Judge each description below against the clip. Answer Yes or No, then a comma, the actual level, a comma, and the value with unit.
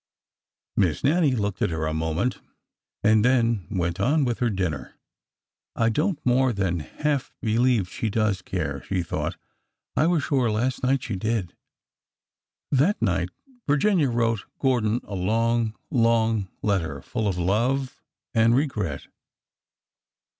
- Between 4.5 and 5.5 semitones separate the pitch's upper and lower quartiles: Yes, average, 5.2 semitones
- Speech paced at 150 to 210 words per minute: No, average, 140 wpm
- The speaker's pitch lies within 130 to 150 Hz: No, low, 115 Hz